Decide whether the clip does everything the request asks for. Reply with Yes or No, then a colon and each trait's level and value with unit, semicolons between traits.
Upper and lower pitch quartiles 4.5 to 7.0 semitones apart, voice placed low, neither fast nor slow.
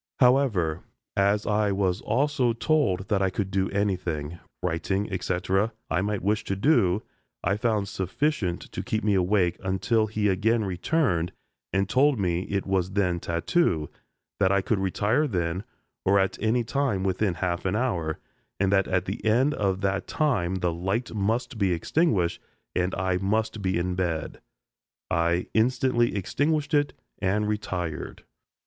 No: average, 3.5 semitones; low, 100 Hz; average, 155 wpm